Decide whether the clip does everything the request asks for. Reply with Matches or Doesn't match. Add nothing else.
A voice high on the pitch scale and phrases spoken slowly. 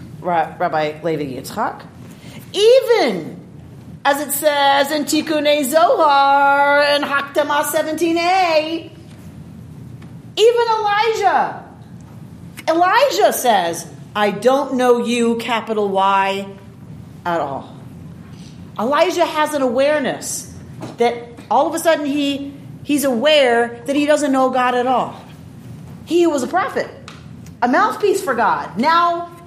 Matches